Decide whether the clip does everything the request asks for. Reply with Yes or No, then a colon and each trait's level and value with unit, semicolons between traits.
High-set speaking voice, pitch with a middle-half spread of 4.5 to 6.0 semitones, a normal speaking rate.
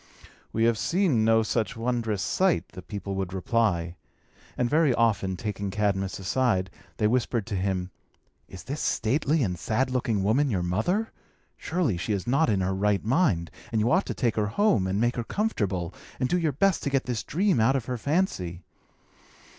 No: low, 110 Hz; wide, 5.6 semitones; average, 185 wpm